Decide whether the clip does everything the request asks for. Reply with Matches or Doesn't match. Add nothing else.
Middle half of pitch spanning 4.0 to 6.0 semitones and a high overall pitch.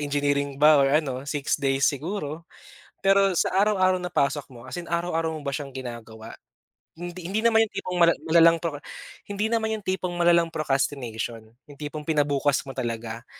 Doesn't match